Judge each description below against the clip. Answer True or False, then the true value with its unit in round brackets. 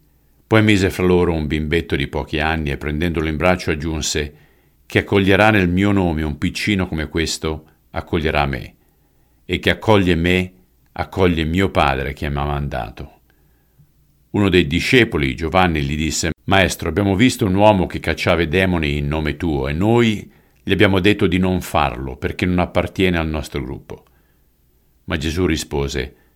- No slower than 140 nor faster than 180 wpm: True (160 wpm)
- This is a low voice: True (85 Hz)